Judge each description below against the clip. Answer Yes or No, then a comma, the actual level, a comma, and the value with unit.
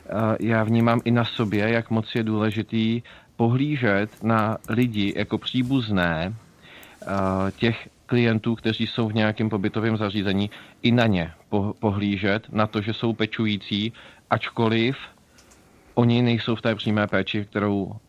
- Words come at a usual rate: Yes, average, 130 wpm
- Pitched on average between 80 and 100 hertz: No, low, 110 Hz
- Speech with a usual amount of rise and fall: No, narrow, 2.0 semitones